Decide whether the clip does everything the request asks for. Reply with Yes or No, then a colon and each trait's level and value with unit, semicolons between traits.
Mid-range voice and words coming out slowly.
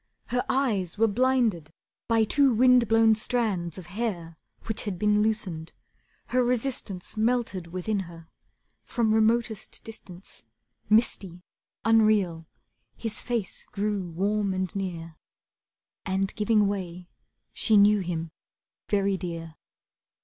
No: high, 205 Hz; slow, 115 wpm